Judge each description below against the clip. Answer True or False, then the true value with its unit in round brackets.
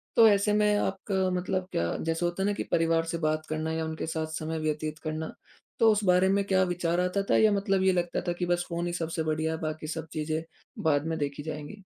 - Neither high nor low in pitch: True (170 Hz)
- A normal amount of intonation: True (3.2 semitones)